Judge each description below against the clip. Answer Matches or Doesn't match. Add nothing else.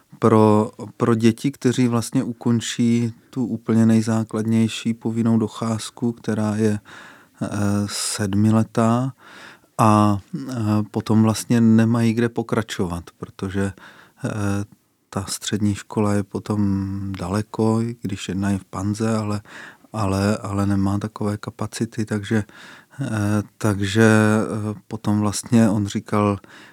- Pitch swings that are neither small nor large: Doesn't match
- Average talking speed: Doesn't match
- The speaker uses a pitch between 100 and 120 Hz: Matches